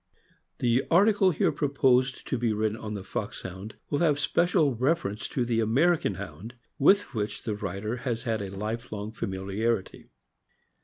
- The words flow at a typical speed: Yes, average, 160 wpm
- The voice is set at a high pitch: No, low, 115 Hz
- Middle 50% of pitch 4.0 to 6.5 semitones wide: Yes, average, 4.7 semitones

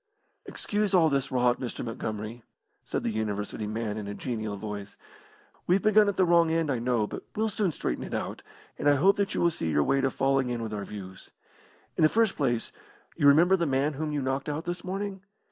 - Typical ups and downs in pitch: No, wide, 7.8 semitones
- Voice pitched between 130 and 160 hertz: Yes, low, 135 Hz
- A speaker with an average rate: No, fast, 220 wpm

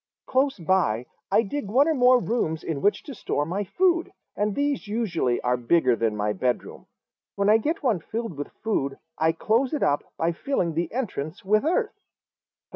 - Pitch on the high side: Yes, high, 205 Hz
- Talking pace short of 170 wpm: No, average, 185 wpm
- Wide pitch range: Yes, wide, 8.5 semitones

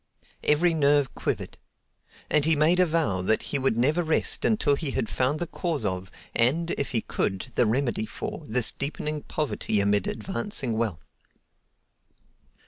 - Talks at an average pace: Yes, average, 155 wpm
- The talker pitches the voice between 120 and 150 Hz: Yes, medium, 140 Hz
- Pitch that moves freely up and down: Yes, wide, 6.0 semitones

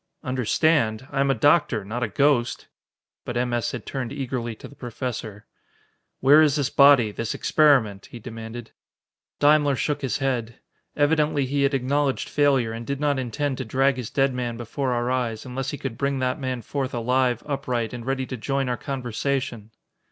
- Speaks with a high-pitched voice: No, low, 130 Hz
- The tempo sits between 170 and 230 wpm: Yes, average, 180 wpm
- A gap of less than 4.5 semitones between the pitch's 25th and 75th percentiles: Yes, average, 2.7 semitones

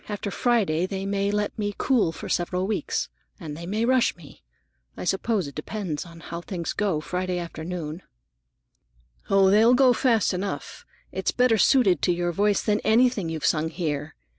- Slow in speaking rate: No, average, 175 wpm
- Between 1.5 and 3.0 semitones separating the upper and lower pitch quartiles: No, average, 4.0 semitones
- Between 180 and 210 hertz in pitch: Yes, high, 190 Hz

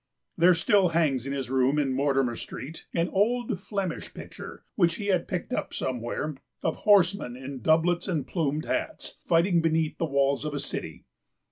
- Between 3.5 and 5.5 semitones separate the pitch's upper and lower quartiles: Yes, average, 4.6 semitones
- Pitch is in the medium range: Yes, medium, 160 Hz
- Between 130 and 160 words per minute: No, average, 170 wpm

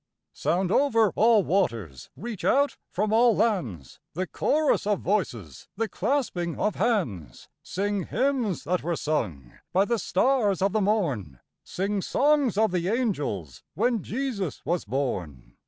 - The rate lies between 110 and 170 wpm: Yes, average, 140 wpm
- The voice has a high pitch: Yes, high, 195 Hz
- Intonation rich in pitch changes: Yes, wide, 7.3 semitones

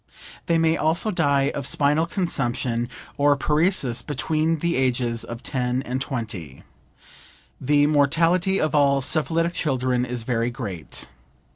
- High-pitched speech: No, medium, 140 Hz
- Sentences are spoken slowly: Yes, slow, 130 wpm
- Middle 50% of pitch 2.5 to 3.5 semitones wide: No, average, 4.5 semitones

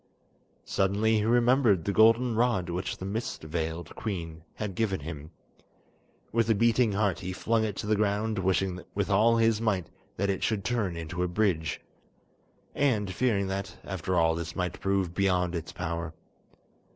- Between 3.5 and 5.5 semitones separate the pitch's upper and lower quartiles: Yes, average, 3.8 semitones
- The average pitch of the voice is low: Yes, low, 100 Hz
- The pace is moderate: Yes, average, 165 wpm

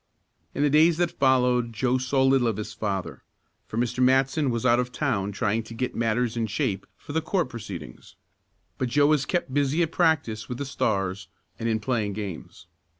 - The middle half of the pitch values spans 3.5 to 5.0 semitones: Yes, average, 4.0 semitones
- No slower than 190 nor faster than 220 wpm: Yes, average, 195 wpm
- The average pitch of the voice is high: No, low, 125 Hz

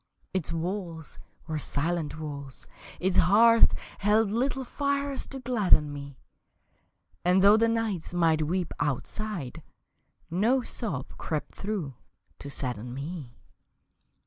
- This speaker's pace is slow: Yes, slow, 115 wpm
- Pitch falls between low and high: Yes, medium, 175 Hz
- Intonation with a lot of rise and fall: Yes, wide, 6.6 semitones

